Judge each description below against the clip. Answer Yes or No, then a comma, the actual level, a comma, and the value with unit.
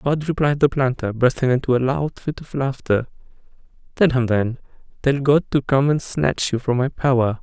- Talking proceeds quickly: No, average, 185 wpm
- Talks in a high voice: No, low, 130 Hz